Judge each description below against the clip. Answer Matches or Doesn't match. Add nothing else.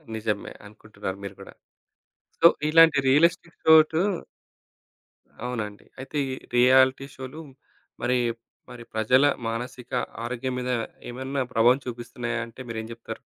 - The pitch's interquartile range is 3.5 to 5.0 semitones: Doesn't match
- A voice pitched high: Doesn't match